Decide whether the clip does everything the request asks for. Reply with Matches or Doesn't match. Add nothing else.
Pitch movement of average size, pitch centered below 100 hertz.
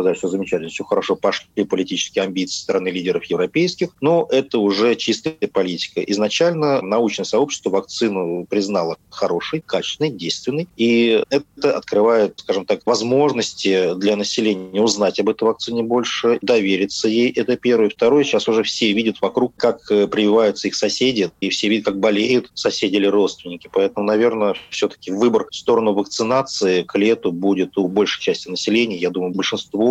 Doesn't match